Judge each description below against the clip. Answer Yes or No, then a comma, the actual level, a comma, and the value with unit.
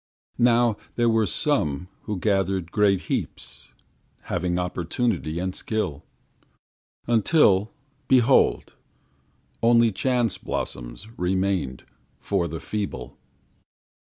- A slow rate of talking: Yes, slow, 90 wpm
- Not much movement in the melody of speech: No, average, 4.7 semitones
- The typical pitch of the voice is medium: No, low, 100 Hz